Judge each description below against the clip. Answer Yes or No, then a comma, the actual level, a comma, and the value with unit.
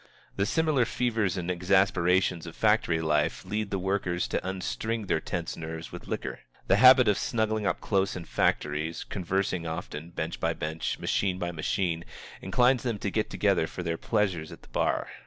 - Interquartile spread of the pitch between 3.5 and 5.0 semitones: Yes, average, 4.1 semitones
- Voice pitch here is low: Yes, very low, 95 Hz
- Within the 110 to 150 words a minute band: No, average, 175 wpm